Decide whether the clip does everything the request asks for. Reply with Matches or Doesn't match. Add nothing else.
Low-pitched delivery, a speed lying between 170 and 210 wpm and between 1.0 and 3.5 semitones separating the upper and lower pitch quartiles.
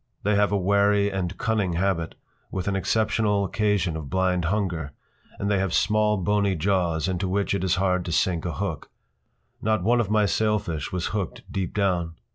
Matches